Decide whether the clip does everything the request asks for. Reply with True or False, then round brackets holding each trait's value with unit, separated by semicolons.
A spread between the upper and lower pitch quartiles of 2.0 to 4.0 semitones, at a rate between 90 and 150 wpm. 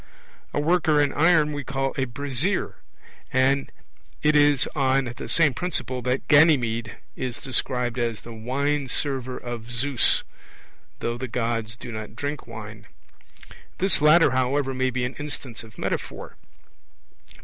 True (3.2 semitones; 140 wpm)